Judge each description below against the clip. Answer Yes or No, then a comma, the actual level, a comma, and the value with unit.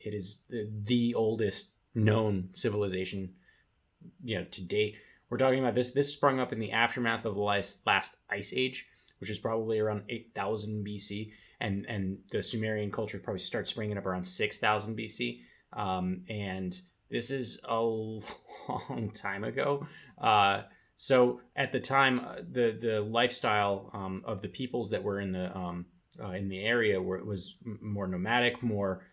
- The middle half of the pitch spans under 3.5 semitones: Yes, average, 3.0 semitones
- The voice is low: Yes, low, 105 Hz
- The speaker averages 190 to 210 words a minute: No, average, 165 wpm